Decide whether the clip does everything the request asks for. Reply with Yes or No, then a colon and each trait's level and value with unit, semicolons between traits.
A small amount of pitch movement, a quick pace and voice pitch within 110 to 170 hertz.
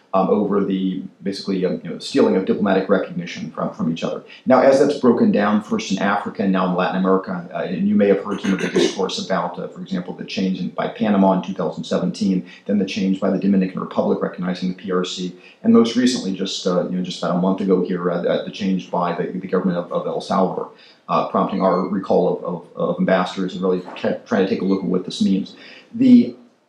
No: narrow, 1.7 semitones; fast, 235 wpm; very low, 95 Hz